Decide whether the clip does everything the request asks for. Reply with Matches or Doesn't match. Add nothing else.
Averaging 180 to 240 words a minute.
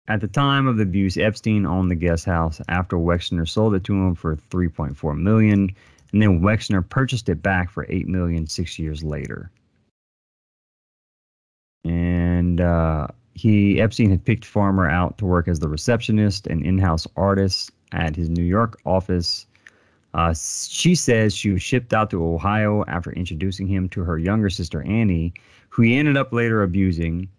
Doesn't match